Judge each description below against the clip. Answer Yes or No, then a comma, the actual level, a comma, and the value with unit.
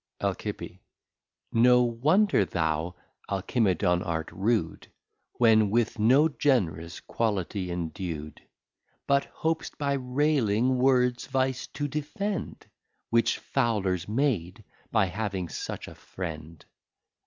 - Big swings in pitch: Yes, wide, 6.5 semitones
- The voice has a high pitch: No, low, 110 Hz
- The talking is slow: Yes, slow, 100 wpm